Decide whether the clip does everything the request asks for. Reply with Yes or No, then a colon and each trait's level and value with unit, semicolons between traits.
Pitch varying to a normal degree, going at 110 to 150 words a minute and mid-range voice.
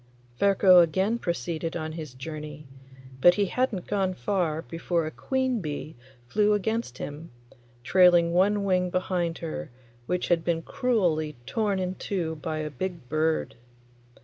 Yes: average, 3.6 semitones; average, 145 wpm; medium, 175 Hz